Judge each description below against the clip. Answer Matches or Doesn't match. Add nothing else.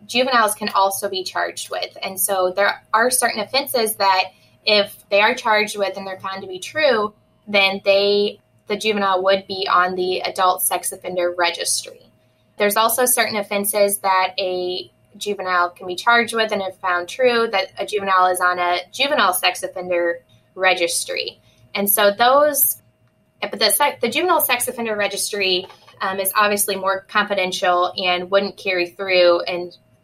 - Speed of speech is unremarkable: Matches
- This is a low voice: Doesn't match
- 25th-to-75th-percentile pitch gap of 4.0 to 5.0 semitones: Doesn't match